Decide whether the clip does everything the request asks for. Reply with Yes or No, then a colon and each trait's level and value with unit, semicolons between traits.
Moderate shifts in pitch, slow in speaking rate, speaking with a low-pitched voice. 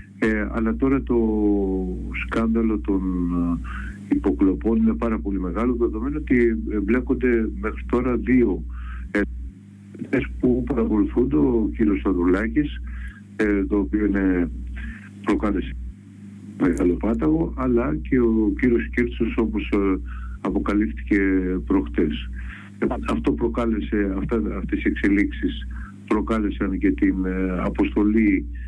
Yes: average, 4.4 semitones; slow, 105 wpm; low, 100 Hz